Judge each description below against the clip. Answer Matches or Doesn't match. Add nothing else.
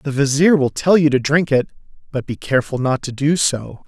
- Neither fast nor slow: Doesn't match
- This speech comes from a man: Matches